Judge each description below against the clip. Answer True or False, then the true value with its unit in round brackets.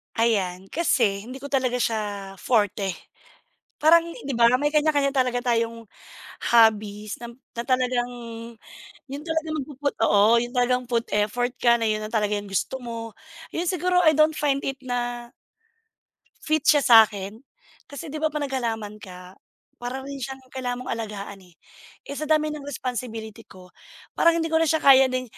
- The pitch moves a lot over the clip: False (4.3 semitones)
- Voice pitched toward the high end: True (245 Hz)